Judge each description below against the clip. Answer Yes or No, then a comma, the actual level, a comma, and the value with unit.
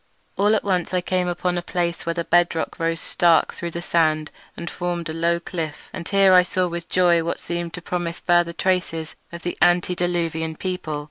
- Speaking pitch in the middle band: Yes, medium, 175 Hz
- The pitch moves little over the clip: Yes, narrow, 1.2 semitones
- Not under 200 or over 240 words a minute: Yes, fast, 205 wpm